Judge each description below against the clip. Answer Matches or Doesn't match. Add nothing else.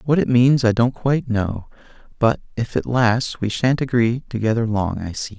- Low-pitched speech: Matches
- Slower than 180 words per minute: Doesn't match